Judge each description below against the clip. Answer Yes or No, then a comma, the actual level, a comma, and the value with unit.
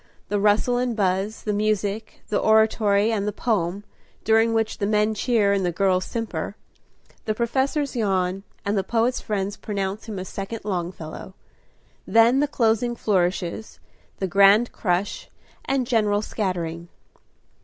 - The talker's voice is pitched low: No, high, 210 Hz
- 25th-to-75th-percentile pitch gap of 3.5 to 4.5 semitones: No, average, 2.7 semitones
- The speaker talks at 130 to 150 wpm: Yes, average, 145 wpm